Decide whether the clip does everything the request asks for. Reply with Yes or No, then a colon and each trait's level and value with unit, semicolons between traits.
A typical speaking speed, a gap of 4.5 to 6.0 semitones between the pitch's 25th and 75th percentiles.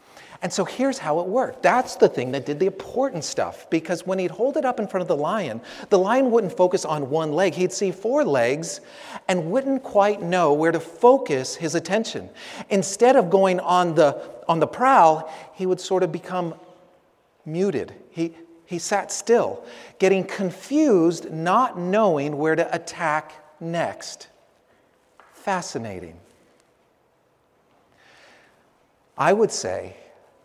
No: average, 150 wpm; average, 3.4 semitones